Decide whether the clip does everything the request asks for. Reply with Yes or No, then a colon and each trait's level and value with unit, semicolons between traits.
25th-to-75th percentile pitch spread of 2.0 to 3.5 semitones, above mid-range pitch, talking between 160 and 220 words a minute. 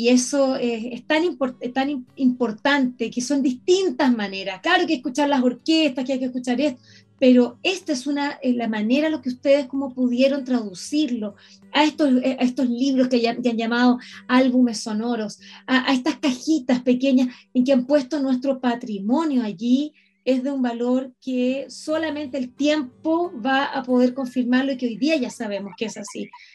Yes: average, 2.7 semitones; very high, 260 Hz; fast, 190 wpm